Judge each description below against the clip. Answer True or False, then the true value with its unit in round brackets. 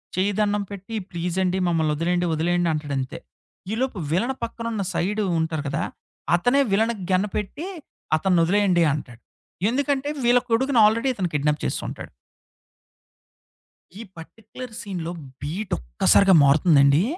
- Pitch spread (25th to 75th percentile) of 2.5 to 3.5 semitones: False (5.2 semitones)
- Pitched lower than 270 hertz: True (185 Hz)